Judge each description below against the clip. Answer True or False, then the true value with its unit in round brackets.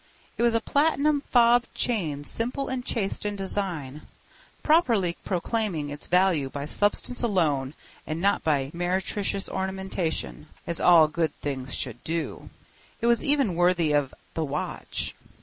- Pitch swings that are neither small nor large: False (6.9 semitones)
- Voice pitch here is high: False (180 Hz)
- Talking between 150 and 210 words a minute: False (135 wpm)